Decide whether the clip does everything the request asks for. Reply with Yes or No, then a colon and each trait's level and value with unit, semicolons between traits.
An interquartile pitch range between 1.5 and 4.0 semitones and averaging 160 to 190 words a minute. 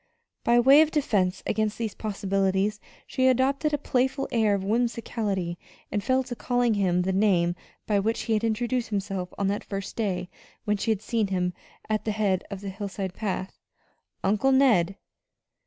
Yes: average, 3.7 semitones; average, 170 wpm